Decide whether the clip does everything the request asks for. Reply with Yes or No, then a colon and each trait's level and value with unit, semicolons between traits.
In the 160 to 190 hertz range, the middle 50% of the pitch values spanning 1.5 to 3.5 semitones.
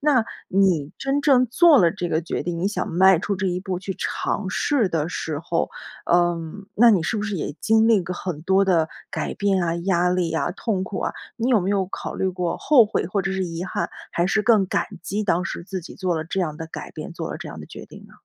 Yes: medium, 185 Hz; average, 3.1 semitones